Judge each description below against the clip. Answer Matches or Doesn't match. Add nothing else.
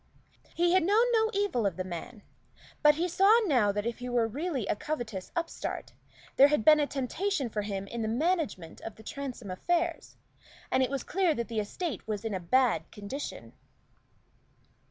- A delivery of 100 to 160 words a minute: Doesn't match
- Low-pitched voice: Doesn't match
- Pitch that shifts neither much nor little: Doesn't match